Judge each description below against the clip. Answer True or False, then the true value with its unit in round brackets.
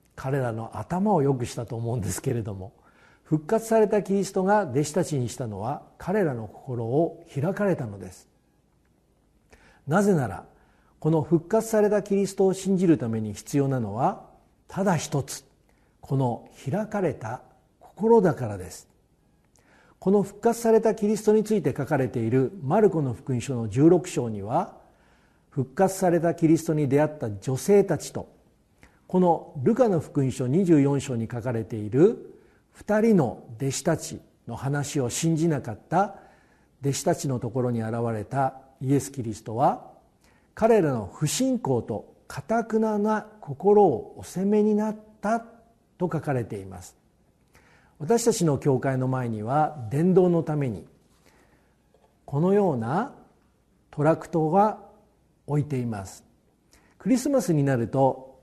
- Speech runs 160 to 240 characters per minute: False (275 characters per minute)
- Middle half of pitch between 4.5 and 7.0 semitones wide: False (7.6 semitones)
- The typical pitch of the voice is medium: True (150 Hz)